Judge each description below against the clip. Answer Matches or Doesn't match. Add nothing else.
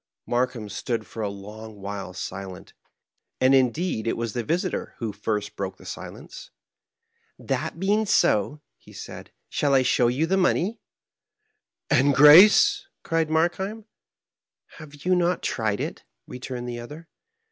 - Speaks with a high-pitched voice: Doesn't match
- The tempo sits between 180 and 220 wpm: Doesn't match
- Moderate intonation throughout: Doesn't match